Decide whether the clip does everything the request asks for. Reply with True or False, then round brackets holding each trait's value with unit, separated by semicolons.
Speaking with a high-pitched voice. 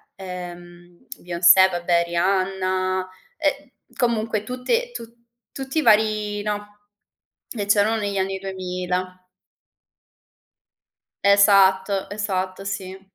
True (195 Hz)